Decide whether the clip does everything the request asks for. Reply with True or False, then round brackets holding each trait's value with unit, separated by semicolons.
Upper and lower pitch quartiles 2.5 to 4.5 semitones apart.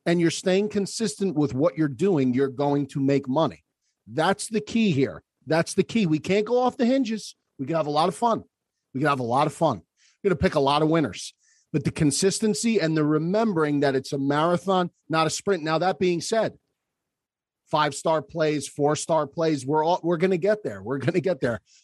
False (5.0 semitones)